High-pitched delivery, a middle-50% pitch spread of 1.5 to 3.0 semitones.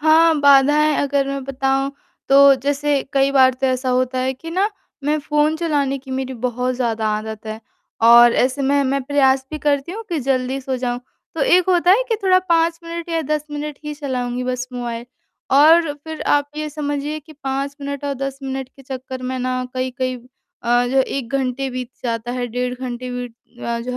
Yes: very high, 270 Hz; narrow, 2.6 semitones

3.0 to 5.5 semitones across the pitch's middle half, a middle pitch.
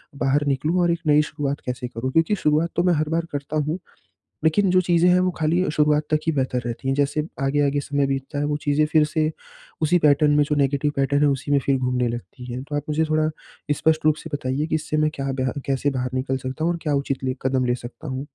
No: narrow, 2.5 semitones; medium, 145 Hz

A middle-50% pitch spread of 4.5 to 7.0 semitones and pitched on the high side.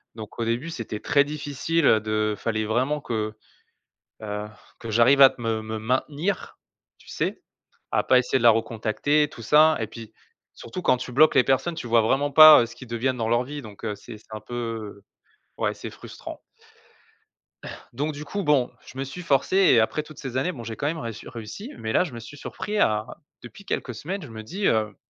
No: average, 4.9 semitones; low, 125 Hz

